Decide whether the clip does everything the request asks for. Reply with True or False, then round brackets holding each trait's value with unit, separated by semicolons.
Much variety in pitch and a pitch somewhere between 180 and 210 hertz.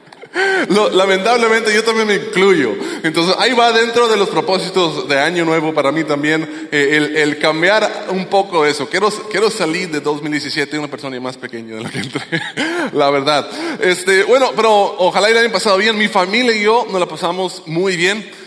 True (6.1 semitones; 185 Hz)